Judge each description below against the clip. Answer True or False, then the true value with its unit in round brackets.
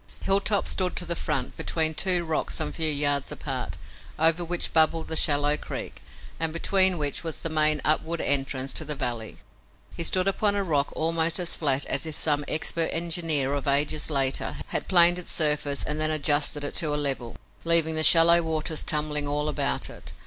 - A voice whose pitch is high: False (155 Hz)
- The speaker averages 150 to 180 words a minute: False (190 wpm)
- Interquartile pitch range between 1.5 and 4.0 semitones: True (2.5 semitones)